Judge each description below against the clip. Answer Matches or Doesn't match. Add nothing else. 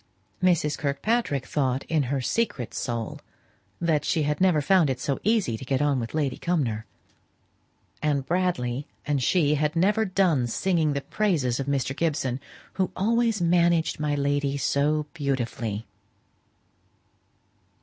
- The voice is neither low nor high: Matches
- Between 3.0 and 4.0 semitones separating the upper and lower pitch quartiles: Doesn't match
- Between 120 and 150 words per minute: Matches